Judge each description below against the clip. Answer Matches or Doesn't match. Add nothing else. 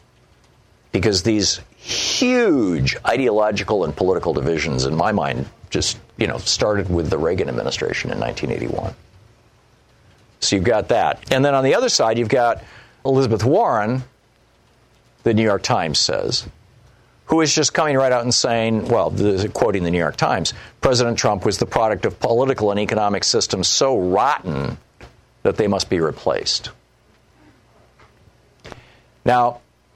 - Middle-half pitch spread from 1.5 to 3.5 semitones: Matches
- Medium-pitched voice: Doesn't match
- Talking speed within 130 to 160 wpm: Matches